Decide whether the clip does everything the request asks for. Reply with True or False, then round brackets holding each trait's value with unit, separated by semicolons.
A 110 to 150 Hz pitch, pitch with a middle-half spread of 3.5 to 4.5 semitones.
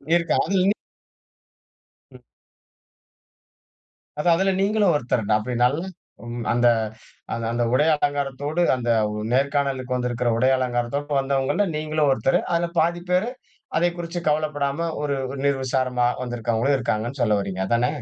True (140 Hz; 4.2 semitones)